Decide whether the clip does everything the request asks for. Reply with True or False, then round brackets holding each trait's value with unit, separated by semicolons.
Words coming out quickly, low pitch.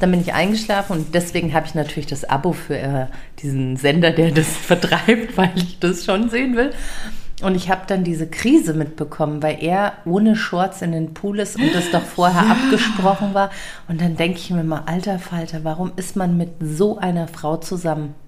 False (195 wpm; 175 Hz)